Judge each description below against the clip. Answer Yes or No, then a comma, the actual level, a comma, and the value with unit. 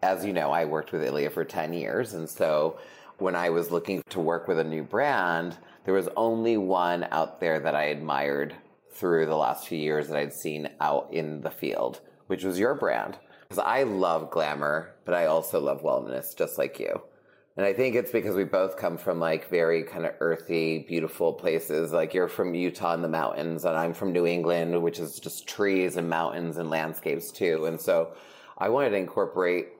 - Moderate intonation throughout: No, narrow, 1.9 semitones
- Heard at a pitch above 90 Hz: No, very low, 85 Hz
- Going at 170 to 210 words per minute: Yes, fast, 205 wpm